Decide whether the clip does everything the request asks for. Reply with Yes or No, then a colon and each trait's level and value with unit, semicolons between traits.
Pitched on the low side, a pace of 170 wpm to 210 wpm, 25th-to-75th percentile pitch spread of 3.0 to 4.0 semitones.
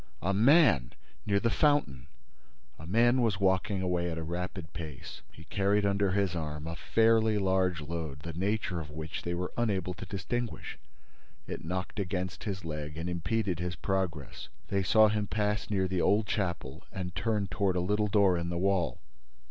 Yes: very low, 95 Hz; average, 175 wpm; average, 3.4 semitones